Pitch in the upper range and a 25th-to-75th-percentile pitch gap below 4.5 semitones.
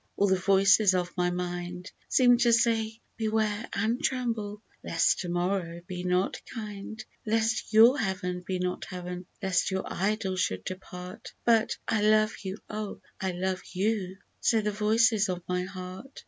Yes: high, 195 Hz; average, 3.3 semitones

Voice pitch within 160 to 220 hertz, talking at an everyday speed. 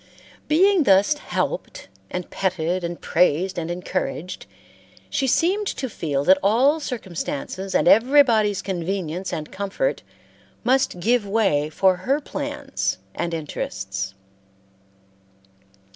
No: high, 190 Hz; slow, 110 wpm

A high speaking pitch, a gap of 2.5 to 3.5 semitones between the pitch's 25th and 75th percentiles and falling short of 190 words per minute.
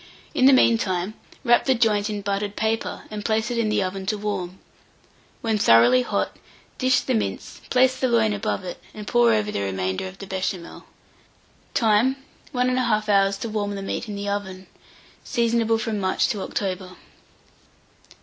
Yes: high, 210 Hz; average, 3.0 semitones; average, 175 wpm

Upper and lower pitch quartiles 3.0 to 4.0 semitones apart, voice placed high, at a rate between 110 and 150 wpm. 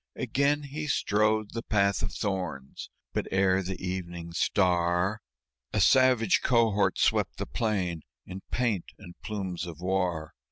No: average, 3.6 semitones; very low, 95 Hz; slow, 135 wpm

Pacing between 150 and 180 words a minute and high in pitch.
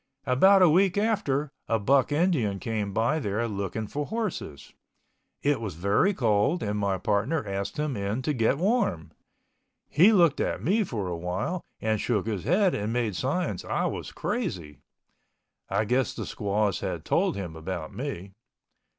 No: average, 165 wpm; low, 115 Hz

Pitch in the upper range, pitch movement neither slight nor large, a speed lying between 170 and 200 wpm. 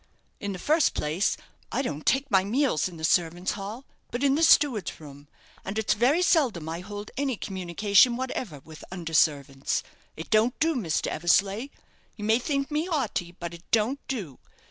No: high, 205 Hz; wide, 7.5 semitones; average, 180 wpm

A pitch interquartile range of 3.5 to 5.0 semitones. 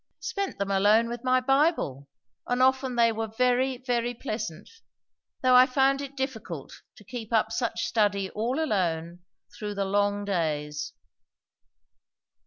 Yes: average, 4.4 semitones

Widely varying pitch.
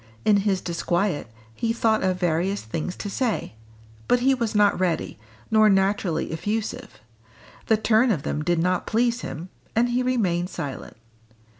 No: average, 4.5 semitones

